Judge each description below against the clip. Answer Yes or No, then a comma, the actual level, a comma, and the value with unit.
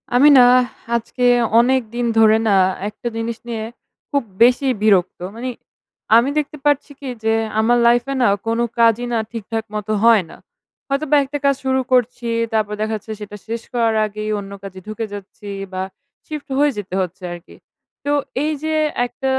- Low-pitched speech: No, high, 230 Hz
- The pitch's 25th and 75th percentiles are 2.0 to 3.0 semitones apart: No, average, 3.4 semitones